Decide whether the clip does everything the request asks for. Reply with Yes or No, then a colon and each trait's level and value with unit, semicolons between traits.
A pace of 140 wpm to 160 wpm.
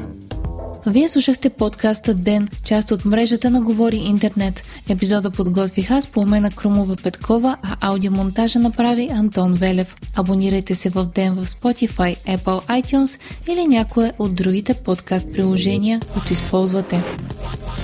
No: average, 125 wpm